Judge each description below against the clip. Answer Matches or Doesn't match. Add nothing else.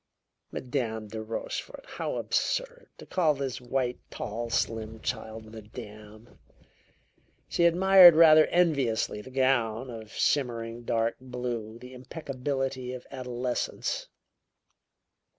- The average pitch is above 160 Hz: Doesn't match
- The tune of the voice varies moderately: Matches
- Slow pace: Matches